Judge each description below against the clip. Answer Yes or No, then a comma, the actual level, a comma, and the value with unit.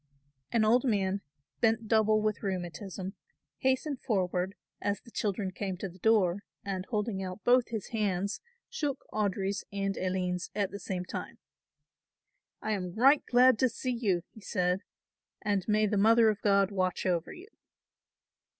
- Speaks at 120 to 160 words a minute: Yes, average, 155 wpm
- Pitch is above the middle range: Yes, high, 200 Hz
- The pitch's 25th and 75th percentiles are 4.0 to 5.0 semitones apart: No, average, 3.0 semitones